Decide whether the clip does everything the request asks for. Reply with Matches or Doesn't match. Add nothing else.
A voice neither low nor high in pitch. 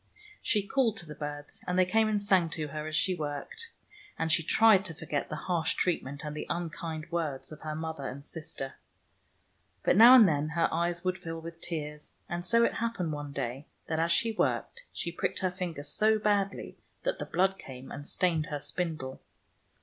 Matches